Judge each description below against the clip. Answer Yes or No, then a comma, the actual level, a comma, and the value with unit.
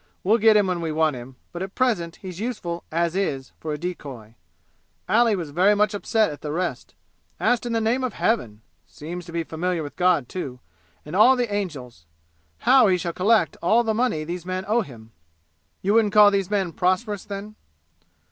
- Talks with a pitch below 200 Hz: Yes, medium, 185 Hz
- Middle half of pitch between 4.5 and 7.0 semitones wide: Yes, average, 4.9 semitones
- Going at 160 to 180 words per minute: No, average, 195 wpm